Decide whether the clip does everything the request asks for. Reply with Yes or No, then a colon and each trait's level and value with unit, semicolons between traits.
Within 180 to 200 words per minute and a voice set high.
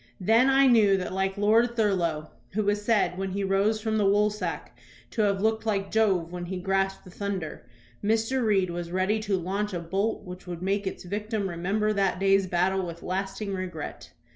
Yes: average, 190 wpm; high, 195 Hz